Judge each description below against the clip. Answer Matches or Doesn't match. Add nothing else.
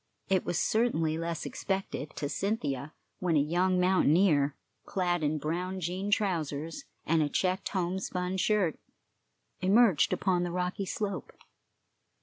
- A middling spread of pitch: Matches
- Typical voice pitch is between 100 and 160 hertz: Doesn't match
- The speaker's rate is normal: Doesn't match